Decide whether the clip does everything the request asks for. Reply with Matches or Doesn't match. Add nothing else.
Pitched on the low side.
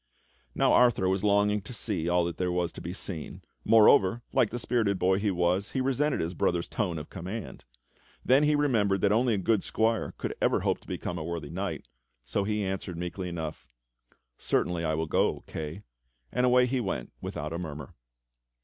Matches